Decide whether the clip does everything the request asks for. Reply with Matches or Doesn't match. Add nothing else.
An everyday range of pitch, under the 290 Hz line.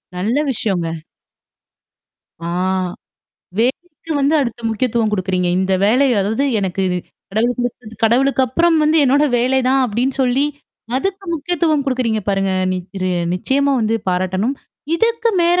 Doesn't match